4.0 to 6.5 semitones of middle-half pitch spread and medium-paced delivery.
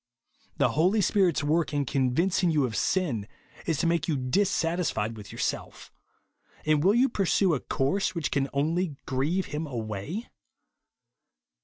Yes: wide, 5.4 semitones; average, 150 wpm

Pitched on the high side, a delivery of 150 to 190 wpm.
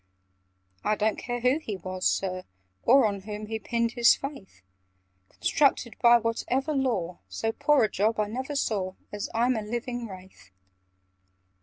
Yes: high, 225 Hz; average, 155 wpm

